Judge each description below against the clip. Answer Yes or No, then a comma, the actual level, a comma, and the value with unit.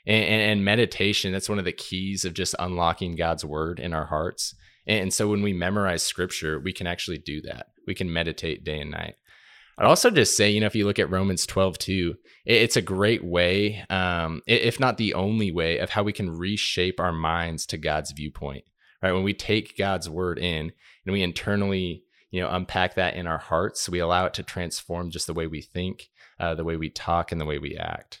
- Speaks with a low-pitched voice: Yes, very low, 90 Hz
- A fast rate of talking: Yes, fast, 220 wpm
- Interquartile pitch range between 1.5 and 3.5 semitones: Yes, average, 2.7 semitones